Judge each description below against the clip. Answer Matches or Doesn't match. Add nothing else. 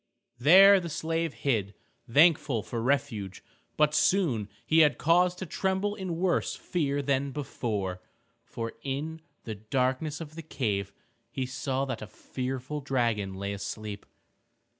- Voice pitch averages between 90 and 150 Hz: Matches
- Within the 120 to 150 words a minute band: Matches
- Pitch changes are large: Matches